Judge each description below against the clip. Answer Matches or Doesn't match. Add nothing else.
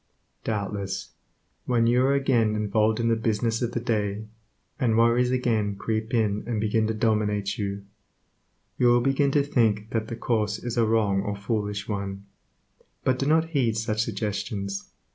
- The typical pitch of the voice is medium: Doesn't match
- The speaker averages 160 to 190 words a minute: Matches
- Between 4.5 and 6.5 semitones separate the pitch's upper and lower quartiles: Doesn't match